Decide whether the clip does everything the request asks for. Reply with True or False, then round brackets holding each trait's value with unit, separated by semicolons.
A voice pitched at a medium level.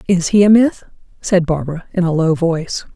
True (175 Hz)